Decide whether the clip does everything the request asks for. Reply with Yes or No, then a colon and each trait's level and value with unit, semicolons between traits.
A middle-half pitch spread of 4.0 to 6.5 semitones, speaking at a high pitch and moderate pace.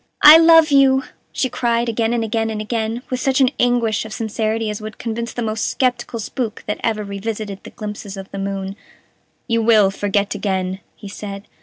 No: average, 2.7 semitones; high, 220 Hz; average, 190 wpm